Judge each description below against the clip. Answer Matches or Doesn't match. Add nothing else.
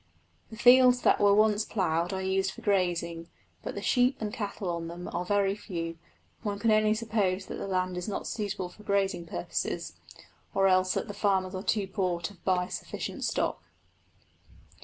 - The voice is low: Doesn't match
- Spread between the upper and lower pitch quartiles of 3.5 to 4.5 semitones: Doesn't match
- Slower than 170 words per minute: Doesn't match